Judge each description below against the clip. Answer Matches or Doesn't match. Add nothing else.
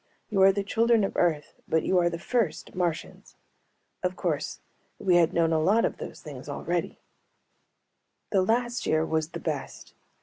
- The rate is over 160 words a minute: Matches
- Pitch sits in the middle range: Matches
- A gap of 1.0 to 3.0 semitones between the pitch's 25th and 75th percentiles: Doesn't match